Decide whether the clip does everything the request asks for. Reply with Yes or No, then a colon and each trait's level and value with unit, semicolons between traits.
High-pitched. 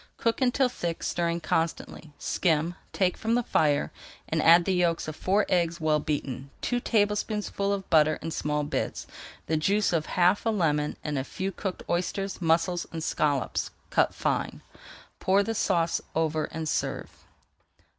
No: medium, 170 Hz